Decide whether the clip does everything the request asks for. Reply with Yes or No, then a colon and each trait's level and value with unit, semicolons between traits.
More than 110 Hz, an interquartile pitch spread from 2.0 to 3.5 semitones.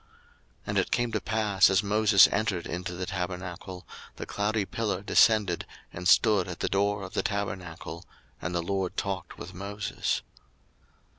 No: very low, 95 Hz; narrow, 2.5 semitones